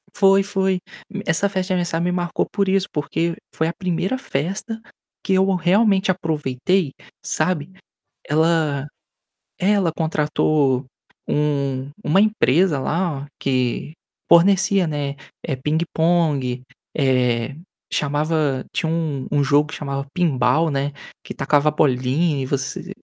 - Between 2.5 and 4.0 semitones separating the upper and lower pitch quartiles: No, average, 4.7 semitones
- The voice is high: No, medium, 160 Hz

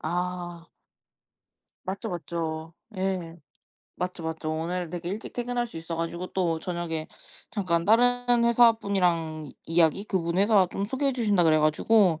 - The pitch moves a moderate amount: Yes, average, 3.9 semitones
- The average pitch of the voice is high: No, medium, 180 Hz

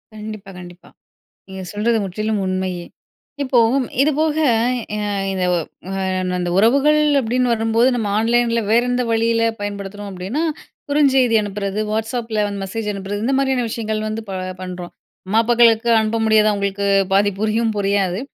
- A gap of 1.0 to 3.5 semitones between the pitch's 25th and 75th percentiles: Yes, average, 3.0 semitones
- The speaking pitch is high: Yes, high, 215 Hz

